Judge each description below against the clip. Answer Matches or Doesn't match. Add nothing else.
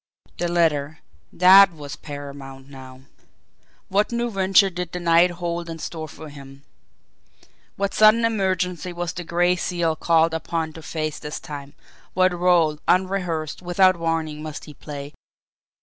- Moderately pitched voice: Matches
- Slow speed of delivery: Doesn't match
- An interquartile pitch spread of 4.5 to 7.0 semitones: Doesn't match